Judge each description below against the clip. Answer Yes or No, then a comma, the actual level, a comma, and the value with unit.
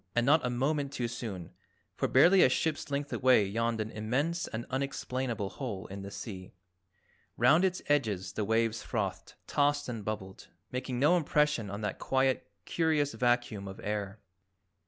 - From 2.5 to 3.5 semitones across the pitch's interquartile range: No, average, 5.1 semitones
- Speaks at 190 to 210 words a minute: No, average, 160 wpm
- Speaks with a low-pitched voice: Yes, low, 125 Hz